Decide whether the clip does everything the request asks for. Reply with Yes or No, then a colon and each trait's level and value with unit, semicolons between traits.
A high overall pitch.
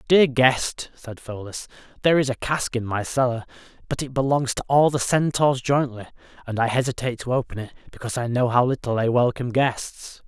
No: low, 125 Hz